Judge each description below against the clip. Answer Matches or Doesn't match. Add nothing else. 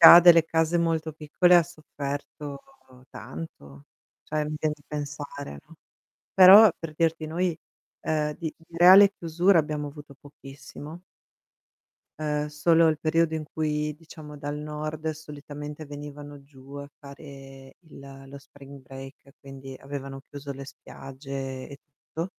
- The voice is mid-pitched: Matches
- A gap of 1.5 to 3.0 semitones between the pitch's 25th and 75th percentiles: Matches